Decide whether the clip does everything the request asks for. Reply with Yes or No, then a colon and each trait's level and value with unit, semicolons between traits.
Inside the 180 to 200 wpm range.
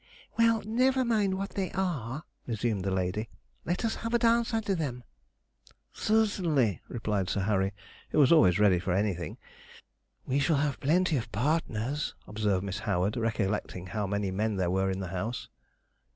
No: average, 165 wpm